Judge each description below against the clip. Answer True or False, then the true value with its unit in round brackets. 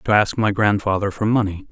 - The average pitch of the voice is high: False (105 Hz)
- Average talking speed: False (210 wpm)